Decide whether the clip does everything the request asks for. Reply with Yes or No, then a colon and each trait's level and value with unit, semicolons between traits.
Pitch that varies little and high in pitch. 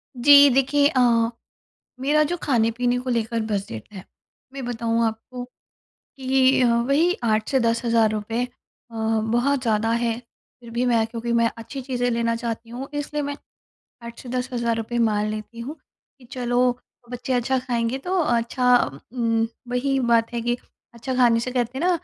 Yes: narrow, 2.1 semitones; high, 240 Hz